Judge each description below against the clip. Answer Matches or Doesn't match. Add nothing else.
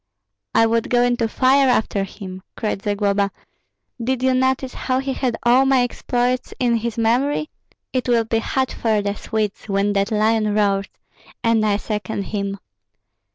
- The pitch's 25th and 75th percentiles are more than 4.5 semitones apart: Doesn't match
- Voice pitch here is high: Matches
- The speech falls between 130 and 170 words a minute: Matches